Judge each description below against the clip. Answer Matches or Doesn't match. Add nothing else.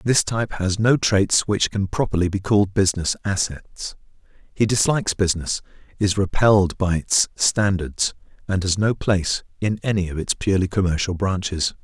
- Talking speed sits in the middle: Matches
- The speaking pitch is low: Matches